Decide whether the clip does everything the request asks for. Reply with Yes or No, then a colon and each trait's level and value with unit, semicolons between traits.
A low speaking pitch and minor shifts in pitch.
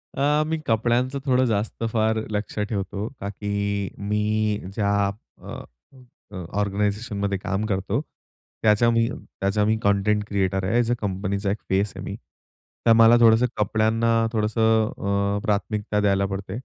Yes: low, 105 Hz; narrow, 2.1 semitones